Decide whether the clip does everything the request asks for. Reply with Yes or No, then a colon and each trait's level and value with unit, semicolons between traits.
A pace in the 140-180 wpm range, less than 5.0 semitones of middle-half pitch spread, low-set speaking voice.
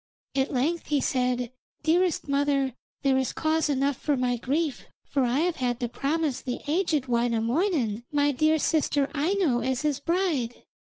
No: average, 160 wpm; average, 3.9 semitones; very high, 280 Hz